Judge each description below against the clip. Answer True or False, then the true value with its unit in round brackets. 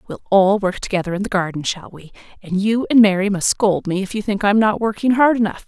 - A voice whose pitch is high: True (205 Hz)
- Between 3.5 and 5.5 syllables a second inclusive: False (5.9 syllables/s)